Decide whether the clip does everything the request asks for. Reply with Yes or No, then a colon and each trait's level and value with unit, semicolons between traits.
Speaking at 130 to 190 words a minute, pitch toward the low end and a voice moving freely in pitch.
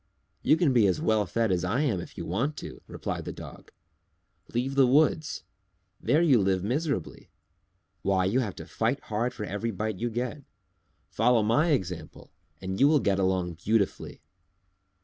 Yes: average, 170 wpm; low, 110 Hz; wide, 6.0 semitones